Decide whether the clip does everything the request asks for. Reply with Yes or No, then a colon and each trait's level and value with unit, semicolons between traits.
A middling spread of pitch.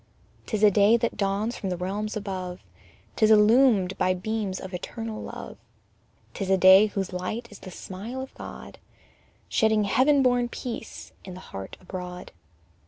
Yes: average, 3.2 semitones